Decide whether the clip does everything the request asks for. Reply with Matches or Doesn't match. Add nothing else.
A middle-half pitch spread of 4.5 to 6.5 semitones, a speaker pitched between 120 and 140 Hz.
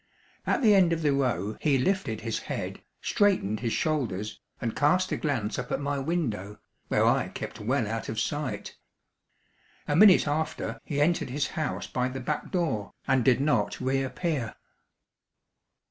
Matches